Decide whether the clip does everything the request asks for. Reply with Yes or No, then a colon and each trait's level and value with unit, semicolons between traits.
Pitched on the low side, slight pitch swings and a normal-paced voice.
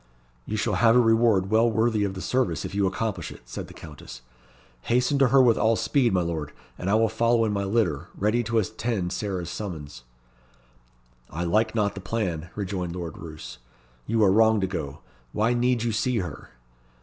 No: low, 105 Hz; average, 4.3 semitones; average, 195 wpm